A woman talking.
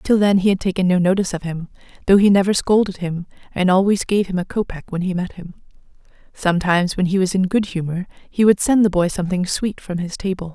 Yes: female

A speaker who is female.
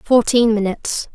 Yes: female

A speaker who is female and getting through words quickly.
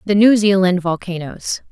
No: female; average, 140 wpm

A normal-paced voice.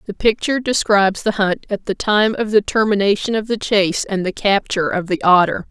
No: fast, 210 wpm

